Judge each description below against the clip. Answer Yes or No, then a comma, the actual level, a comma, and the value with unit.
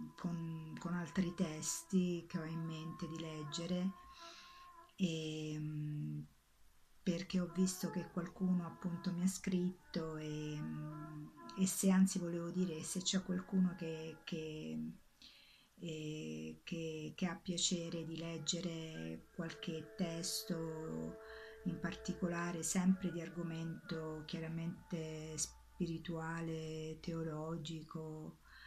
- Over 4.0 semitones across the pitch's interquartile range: No, narrow, 2.5 semitones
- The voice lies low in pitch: No, medium, 165 Hz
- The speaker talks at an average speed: No, slow, 100 wpm